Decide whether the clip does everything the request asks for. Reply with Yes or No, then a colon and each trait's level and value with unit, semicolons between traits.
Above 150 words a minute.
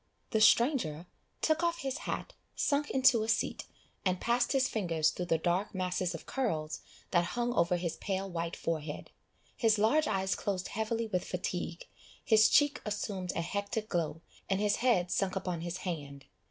Yes: average, 170 wpm